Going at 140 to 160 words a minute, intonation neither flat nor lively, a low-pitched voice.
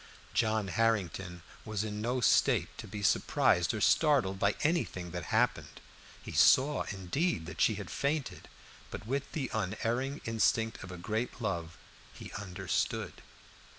Yes: average, 145 wpm; average, 4.8 semitones; low, 110 Hz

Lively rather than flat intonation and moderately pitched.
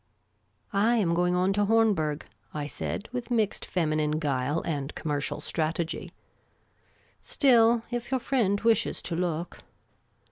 Yes: wide, 6.5 semitones; medium, 180 Hz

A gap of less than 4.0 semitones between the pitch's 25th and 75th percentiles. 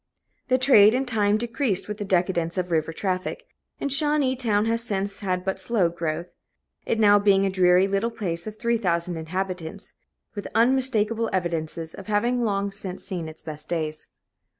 No: average, 4.4 semitones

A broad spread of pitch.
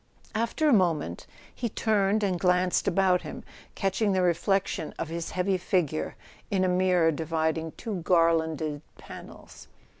No: average, 3.1 semitones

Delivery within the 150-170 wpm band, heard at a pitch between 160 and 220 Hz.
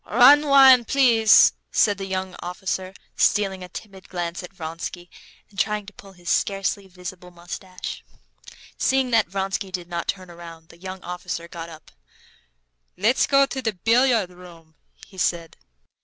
Yes: average, 155 wpm; high, 190 Hz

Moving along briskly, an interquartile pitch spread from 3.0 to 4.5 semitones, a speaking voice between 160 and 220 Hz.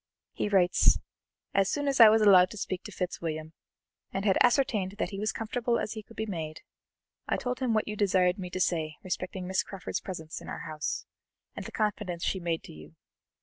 Yes: fast, 210 wpm; average, 3.3 semitones; high, 190 Hz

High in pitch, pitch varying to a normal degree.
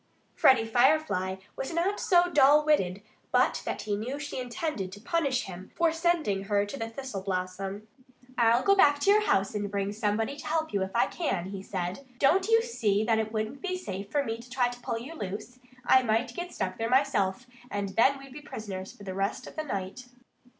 No: high, 230 Hz; wide, 6.6 semitones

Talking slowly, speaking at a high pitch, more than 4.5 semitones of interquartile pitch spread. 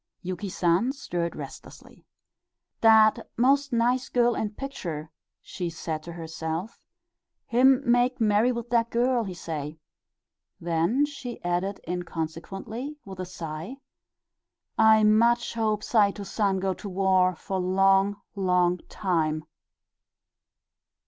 Yes: slow, 115 wpm; high, 200 Hz; average, 5.0 semitones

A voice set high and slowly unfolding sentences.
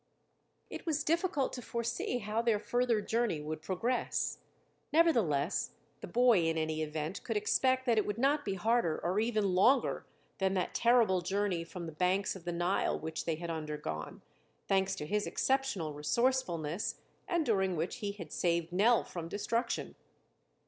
No: high, 200 Hz; average, 165 wpm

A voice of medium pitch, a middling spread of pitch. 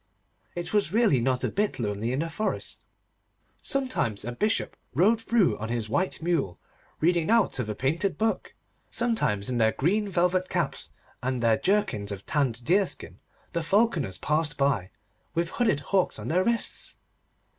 No: medium, 165 Hz; wide, 9.0 semitones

